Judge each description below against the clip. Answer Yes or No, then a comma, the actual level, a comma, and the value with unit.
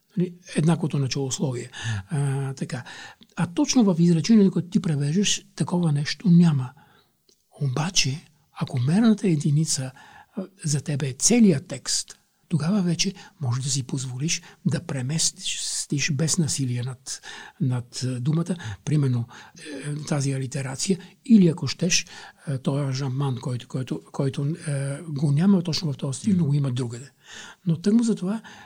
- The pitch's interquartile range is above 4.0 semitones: Yes, average, 4.5 semitones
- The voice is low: No, medium, 155 Hz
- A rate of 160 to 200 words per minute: No, average, 135 wpm